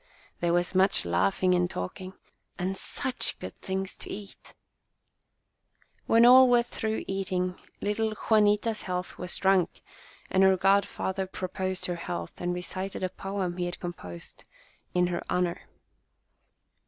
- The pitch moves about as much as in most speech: No, narrow, 1.9 semitones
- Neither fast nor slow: Yes, average, 155 wpm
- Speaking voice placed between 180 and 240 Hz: Yes, medium, 185 Hz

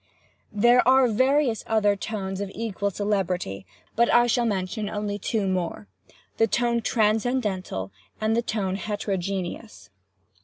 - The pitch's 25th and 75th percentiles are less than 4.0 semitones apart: Yes, average, 3.3 semitones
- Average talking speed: No, slow, 120 wpm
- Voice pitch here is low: No, high, 210 Hz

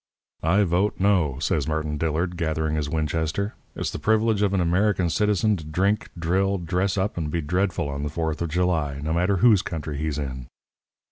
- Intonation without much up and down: No, average, 4.0 semitones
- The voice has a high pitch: No, very low, 85 Hz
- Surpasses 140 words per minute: Yes, average, 190 wpm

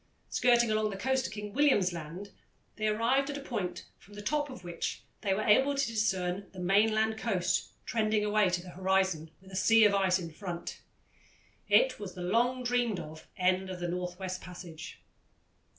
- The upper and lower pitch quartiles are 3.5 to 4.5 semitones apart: Yes, average, 3.8 semitones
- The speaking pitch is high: Yes, high, 205 Hz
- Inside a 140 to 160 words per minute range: No, average, 190 wpm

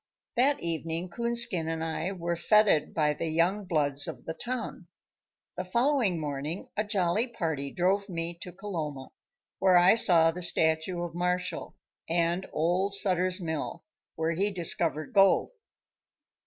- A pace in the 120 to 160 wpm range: Yes, average, 140 wpm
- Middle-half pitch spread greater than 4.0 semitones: No, average, 3.4 semitones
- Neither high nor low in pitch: Yes, medium, 175 Hz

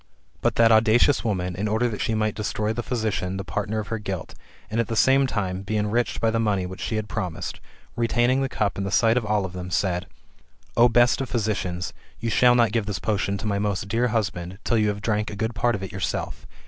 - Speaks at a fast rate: Yes, fast, 240 wpm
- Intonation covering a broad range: No, average, 2.7 semitones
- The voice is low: Yes, low, 105 Hz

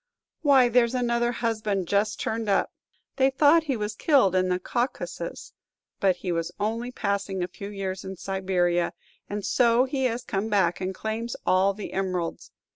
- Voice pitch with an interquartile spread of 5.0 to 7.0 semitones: No, average, 4.1 semitones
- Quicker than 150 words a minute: Yes, average, 170 wpm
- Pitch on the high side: Yes, high, 205 Hz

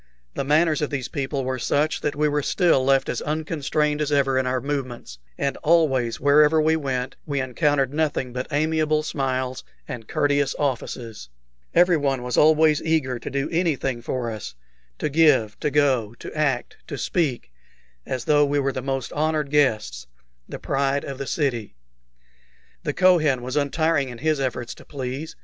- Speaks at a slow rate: No, average, 170 wpm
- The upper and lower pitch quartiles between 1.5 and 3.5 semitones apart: Yes, average, 2.9 semitones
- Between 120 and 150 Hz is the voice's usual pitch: Yes, medium, 140 Hz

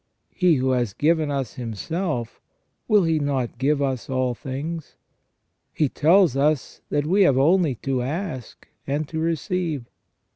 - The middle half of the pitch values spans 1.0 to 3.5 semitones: No, average, 4.1 semitones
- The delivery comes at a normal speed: Yes, average, 145 wpm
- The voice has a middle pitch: Yes, medium, 145 Hz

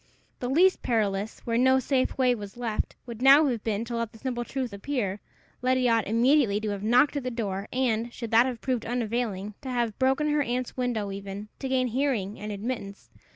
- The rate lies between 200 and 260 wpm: Yes, fast, 205 wpm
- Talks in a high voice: Yes, high, 240 Hz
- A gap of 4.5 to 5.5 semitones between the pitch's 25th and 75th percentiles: No, average, 3.3 semitones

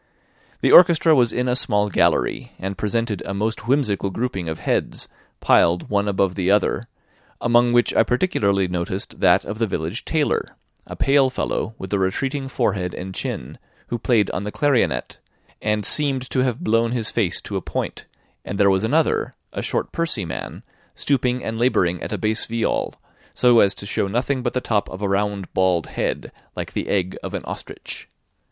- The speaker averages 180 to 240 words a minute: Yes, average, 185 wpm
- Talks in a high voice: No, low, 110 Hz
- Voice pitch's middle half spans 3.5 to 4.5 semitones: Yes, average, 4.2 semitones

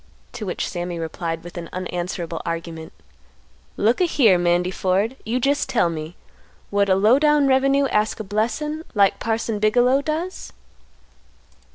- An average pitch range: No, wide, 6.6 semitones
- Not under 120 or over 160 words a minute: Yes, average, 150 wpm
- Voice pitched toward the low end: No, high, 205 Hz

